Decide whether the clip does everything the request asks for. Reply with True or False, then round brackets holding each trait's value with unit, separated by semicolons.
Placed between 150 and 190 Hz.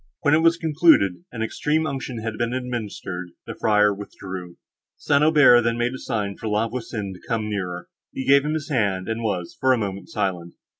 False (115 Hz)